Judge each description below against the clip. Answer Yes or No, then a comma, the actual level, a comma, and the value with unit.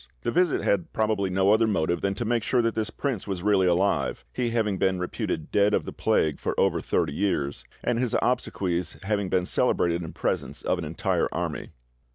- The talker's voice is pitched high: No, low, 100 Hz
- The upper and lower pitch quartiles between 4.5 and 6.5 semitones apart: No, average, 3.9 semitones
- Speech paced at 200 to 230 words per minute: Yes, fast, 205 wpm